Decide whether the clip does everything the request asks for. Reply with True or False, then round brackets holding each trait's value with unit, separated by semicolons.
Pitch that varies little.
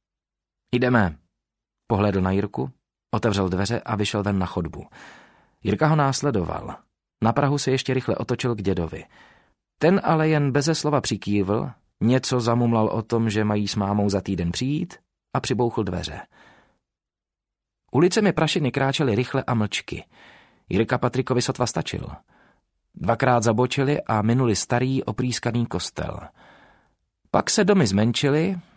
False (4.6 semitones)